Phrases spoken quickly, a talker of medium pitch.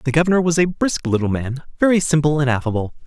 Yes: fast, 215 wpm; medium, 150 Hz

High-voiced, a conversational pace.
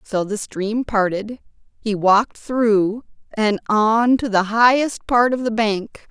Yes: high, 220 Hz; average, 155 wpm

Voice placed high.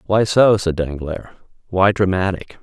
No: very low, 95 Hz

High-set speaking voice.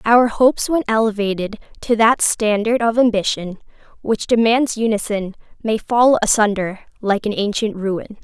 Yes: high, 220 Hz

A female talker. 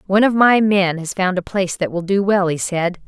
Yes: female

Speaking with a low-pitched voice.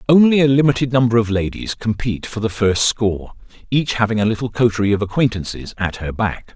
Yes: low, 110 Hz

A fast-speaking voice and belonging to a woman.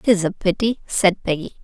Yes: fast, 220 wpm; female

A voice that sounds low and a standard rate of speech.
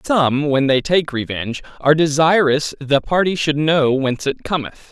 No: medium, 145 Hz; average, 170 wpm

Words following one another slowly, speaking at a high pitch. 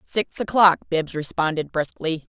No: slow, 130 wpm; medium, 170 Hz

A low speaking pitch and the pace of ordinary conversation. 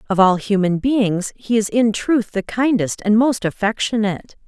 No: high, 215 Hz; average, 175 wpm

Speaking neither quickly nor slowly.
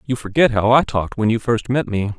No: fast, 275 wpm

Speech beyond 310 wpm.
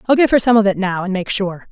Yes: fast, 350 wpm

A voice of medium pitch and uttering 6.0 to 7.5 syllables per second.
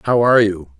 No: low, 110 Hz; 6.4 syllables/s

